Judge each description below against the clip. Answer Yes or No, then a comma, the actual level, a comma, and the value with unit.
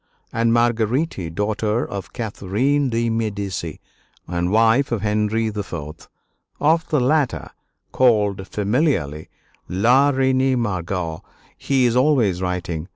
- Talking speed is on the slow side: Yes, slow, 110 wpm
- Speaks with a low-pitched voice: Yes, low, 110 Hz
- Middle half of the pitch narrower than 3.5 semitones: No, average, 5.1 semitones